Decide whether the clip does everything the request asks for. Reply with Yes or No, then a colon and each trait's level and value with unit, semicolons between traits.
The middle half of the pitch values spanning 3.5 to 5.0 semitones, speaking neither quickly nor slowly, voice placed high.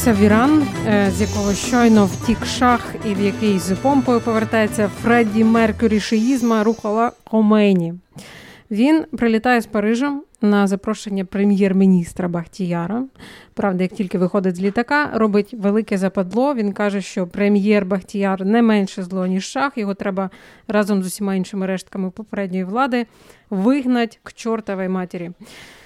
No: average, 2.9 semitones; average, 130 wpm; high, 210 Hz